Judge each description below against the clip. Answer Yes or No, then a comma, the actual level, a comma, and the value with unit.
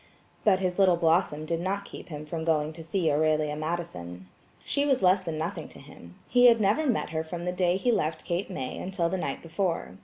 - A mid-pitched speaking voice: Yes, medium, 170 Hz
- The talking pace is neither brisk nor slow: No, fast, 220 wpm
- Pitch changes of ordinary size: Yes, average, 3.4 semitones